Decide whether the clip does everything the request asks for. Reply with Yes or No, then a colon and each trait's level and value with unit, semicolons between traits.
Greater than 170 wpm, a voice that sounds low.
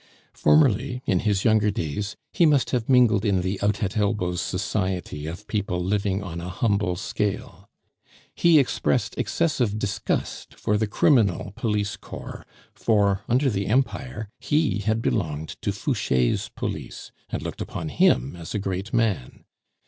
No: average, 150 wpm; low, 105 Hz